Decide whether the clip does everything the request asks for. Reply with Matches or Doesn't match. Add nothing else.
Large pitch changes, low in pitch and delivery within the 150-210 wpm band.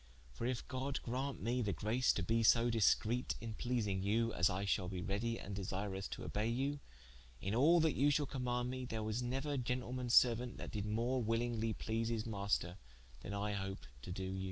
Doesn't match